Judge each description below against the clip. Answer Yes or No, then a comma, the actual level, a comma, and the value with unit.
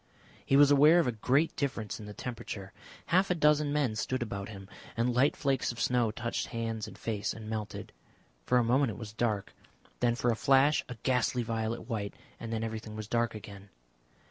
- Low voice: Yes, low, 115 Hz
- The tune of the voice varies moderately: Yes, average, 3.5 semitones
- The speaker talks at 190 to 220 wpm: Yes, average, 200 wpm